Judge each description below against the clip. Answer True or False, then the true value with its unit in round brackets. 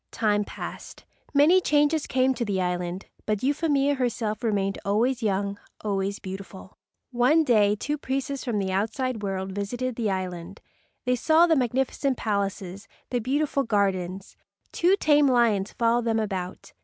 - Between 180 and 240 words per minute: False (145 wpm)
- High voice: True (225 Hz)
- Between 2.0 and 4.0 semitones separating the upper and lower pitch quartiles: False (5.1 semitones)